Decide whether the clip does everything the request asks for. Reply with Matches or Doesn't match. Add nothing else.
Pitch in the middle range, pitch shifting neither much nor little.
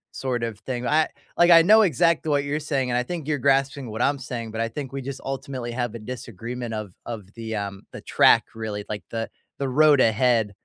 Doesn't match